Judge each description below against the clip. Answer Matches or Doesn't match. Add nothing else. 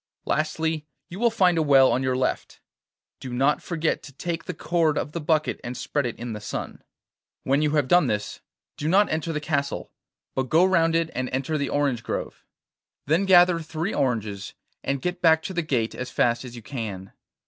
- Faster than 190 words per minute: Matches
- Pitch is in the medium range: Matches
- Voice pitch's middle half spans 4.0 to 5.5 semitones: Matches